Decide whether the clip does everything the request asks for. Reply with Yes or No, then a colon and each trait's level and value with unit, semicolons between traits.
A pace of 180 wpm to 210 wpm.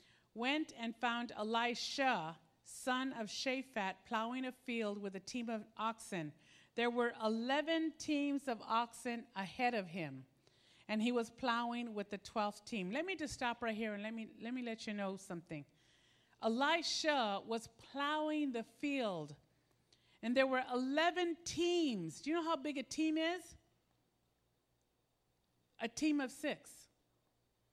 No: average, 150 wpm